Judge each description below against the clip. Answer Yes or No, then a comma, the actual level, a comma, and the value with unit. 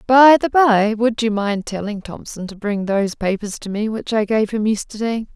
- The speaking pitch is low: No, high, 215 Hz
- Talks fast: Yes, fast, 215 wpm